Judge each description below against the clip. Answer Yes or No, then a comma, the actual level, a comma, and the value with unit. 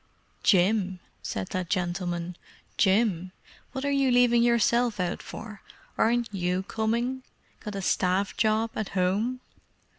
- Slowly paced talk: Yes, slow, 125 wpm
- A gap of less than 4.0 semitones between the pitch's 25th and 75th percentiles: No, average, 4.4 semitones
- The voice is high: Yes, high, 210 Hz